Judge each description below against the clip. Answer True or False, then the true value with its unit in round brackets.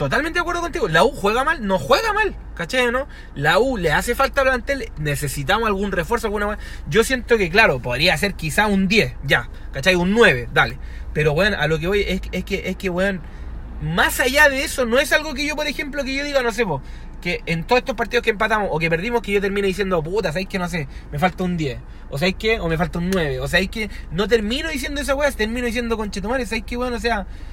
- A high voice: True (205 Hz)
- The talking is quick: True (245 wpm)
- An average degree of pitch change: False (6.0 semitones)